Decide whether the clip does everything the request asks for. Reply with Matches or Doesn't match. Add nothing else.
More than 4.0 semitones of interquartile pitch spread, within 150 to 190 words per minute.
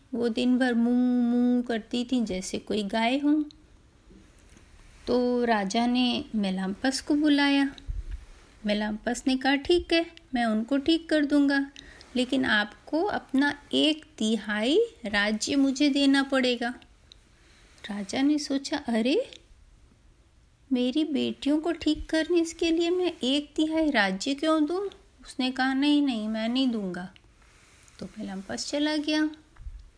Doesn't match